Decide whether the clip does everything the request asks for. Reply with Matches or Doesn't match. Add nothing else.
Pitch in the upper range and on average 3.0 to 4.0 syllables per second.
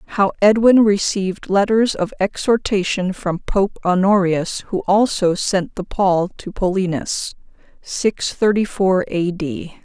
Matches